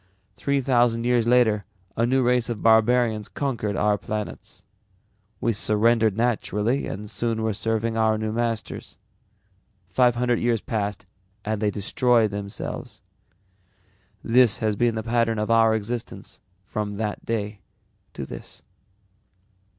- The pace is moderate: No, slow, 130 wpm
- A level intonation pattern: Yes, narrow, 2.0 semitones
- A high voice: No, low, 115 Hz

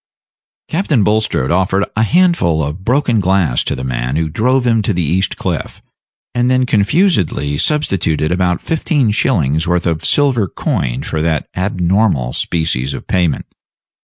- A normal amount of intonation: No, wide, 7.3 semitones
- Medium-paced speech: Yes, average, 150 wpm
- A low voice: Yes, very low, 95 Hz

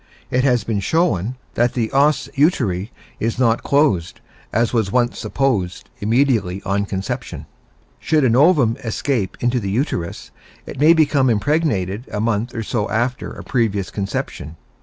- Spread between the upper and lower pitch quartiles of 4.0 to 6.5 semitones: Yes, average, 4.9 semitones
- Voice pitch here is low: Yes, low, 115 Hz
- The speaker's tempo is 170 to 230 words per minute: No, average, 150 wpm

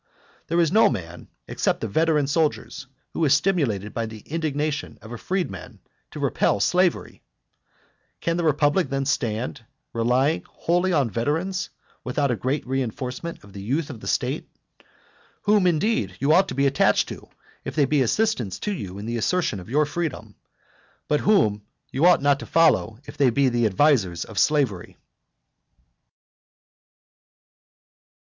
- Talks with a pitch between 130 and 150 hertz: Yes, medium, 140 Hz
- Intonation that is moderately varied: No, wide, 6.1 semitones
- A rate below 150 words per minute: No, average, 155 wpm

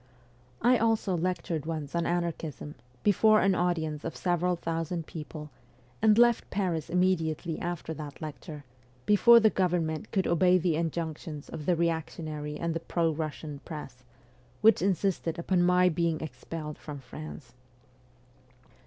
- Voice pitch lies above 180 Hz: No, medium, 165 Hz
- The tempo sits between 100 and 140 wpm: Yes, slow, 135 wpm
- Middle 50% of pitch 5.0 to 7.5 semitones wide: No, narrow, 2.6 semitones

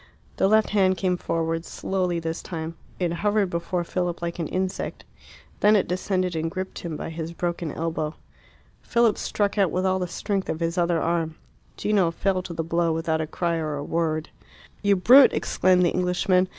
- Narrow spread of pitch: Yes, narrow, 2.3 semitones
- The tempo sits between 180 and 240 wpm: Yes, average, 190 wpm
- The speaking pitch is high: No, medium, 175 Hz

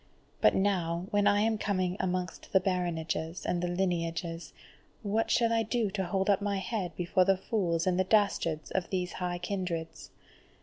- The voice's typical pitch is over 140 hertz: Yes, medium, 185 Hz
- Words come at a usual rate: Yes, average, 175 wpm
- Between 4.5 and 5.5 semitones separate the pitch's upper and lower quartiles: No, narrow, 2.6 semitones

